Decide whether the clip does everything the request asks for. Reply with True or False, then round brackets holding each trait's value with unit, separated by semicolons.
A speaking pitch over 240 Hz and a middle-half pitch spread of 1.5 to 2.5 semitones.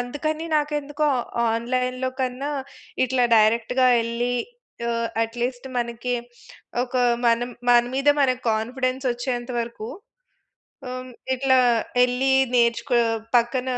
True (250 Hz; 1.8 semitones)